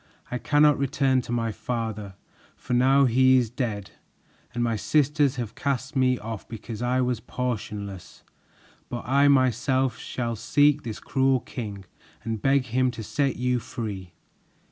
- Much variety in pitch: No, average, 2.9 semitones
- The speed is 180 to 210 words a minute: No, average, 150 wpm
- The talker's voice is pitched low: Yes, low, 125 Hz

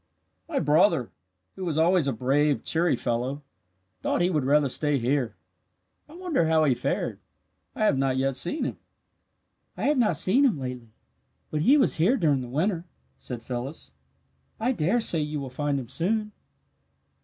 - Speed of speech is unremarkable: Yes, average, 170 wpm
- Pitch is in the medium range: Yes, medium, 150 Hz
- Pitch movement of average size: No, wide, 5.9 semitones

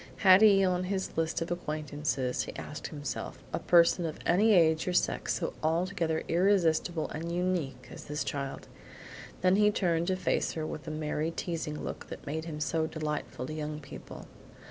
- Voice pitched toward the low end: No, medium, 165 Hz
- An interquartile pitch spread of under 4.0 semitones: Yes, average, 2.9 semitones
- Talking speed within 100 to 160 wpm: No, average, 180 wpm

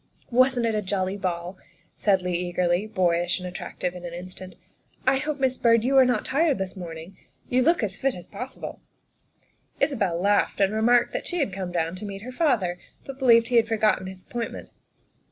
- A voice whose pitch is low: No, high, 205 Hz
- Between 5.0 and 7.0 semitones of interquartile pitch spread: Yes, wide, 5.5 semitones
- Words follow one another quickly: Yes, fast, 215 wpm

